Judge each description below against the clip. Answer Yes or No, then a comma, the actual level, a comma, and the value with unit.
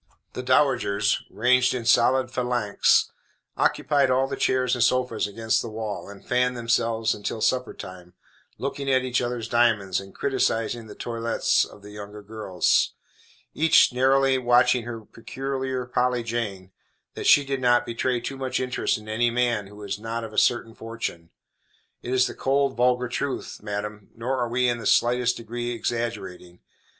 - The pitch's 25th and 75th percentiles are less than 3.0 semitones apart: Yes, narrow, 2.6 semitones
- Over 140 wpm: Yes, average, 165 wpm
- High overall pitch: No, low, 120 Hz